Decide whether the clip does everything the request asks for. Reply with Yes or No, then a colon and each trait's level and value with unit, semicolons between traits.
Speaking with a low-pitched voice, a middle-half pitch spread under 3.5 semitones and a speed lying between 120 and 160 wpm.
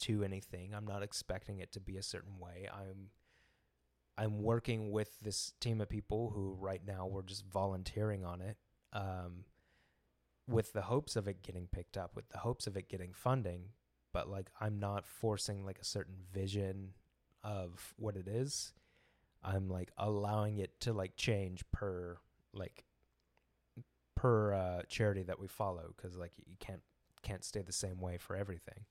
No: very low, 95 Hz; narrow, 2.6 semitones; average, 170 wpm